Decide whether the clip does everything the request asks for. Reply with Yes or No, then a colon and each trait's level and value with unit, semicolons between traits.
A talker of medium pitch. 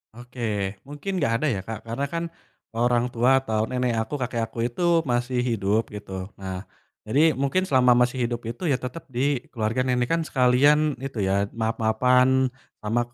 No: low, 125 Hz